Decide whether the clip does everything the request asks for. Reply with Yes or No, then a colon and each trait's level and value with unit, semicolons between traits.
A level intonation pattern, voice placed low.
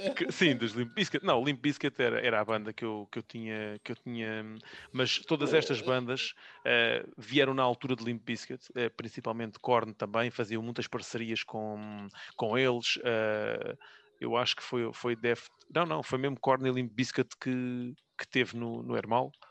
Yes: narrow, 2.3 semitones; low, 120 Hz